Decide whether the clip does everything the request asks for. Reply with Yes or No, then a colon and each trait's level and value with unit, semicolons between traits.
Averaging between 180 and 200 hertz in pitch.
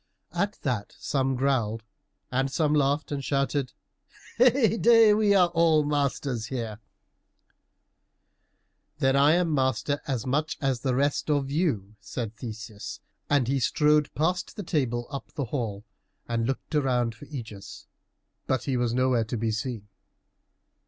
No: low, 135 Hz